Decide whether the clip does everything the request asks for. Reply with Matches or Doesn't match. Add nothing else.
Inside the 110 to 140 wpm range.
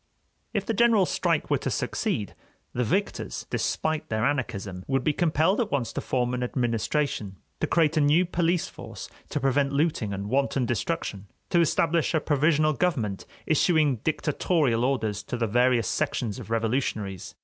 Doesn't match